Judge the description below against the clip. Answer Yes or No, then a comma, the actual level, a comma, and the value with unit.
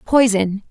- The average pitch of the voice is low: No, high, 215 Hz